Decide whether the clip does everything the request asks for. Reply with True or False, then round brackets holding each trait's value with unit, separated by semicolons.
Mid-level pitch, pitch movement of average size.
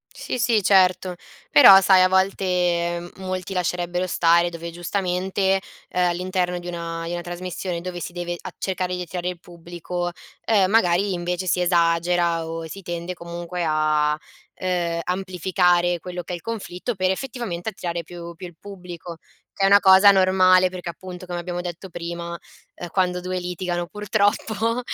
False (180 Hz; 1.4 semitones)